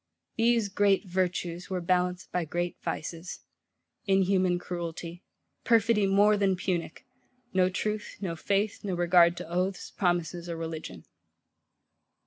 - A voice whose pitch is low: No, medium, 180 Hz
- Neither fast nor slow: No, slow, 120 wpm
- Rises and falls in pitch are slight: Yes, narrow, 2.3 semitones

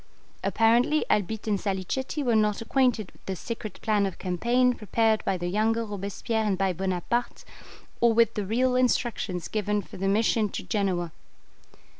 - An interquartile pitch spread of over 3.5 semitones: No, average, 3.2 semitones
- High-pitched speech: Yes, high, 215 Hz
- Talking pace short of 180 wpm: Yes, average, 160 wpm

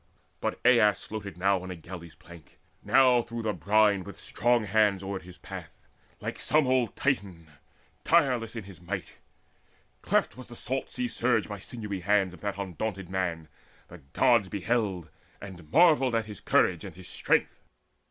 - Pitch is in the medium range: No, low, 100 Hz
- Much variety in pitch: No, average, 4.2 semitones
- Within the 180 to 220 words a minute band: No, average, 170 wpm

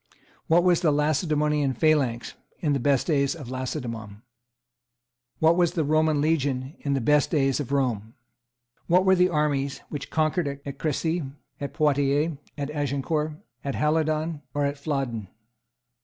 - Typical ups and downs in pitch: No, narrow, 2.3 semitones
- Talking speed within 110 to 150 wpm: Yes, average, 145 wpm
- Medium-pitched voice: Yes, medium, 145 Hz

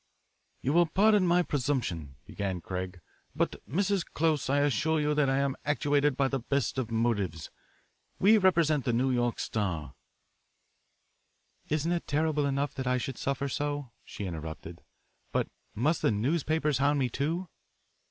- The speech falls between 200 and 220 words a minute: No, average, 155 wpm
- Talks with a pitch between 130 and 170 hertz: Yes, medium, 140 Hz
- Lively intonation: No, average, 4.6 semitones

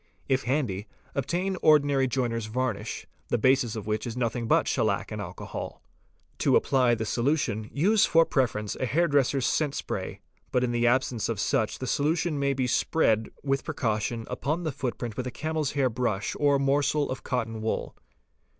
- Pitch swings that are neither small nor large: Yes, average, 3.6 semitones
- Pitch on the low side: Yes, low, 130 Hz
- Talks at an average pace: Yes, average, 170 wpm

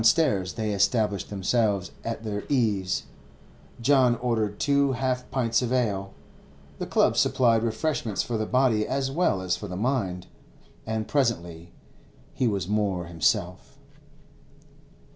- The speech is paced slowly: Yes, slow, 125 wpm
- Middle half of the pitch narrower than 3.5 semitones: No, average, 4.4 semitones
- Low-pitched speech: Yes, low, 110 Hz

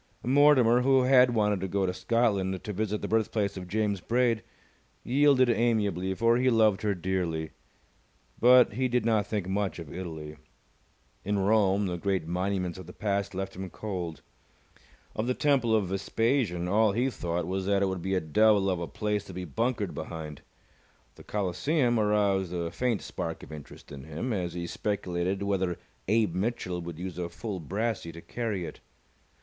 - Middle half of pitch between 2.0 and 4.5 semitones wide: Yes, average, 4.0 semitones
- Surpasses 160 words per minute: Yes, average, 175 wpm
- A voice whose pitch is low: Yes, low, 100 Hz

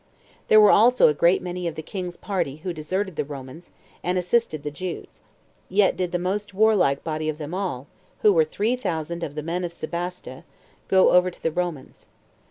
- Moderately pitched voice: Yes, medium, 175 Hz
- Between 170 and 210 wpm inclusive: Yes, average, 195 wpm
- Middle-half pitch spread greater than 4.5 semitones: No, average, 3.4 semitones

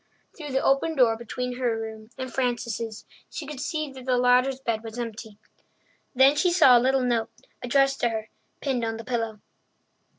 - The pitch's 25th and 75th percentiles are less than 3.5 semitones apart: Yes, average, 2.9 semitones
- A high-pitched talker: Yes, very high, 250 Hz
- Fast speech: No, average, 185 wpm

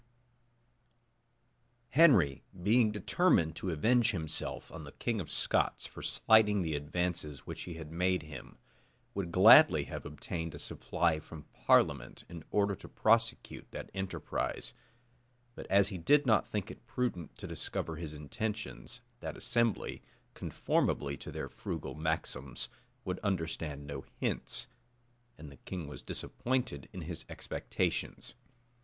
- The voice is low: Yes, very low, 90 Hz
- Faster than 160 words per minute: No, slow, 135 wpm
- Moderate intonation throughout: No, wide, 6.2 semitones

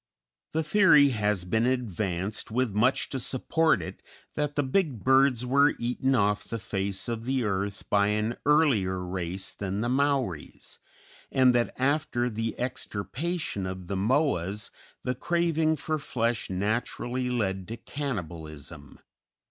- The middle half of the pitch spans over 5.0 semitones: Yes, wide, 5.6 semitones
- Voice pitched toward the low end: Yes, low, 120 Hz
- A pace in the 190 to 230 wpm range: No, average, 140 wpm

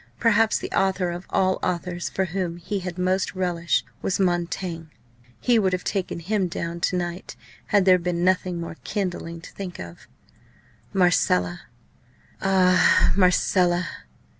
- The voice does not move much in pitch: Yes, narrow, 1.6 semitones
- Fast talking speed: No, average, 140 wpm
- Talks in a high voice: No, medium, 180 Hz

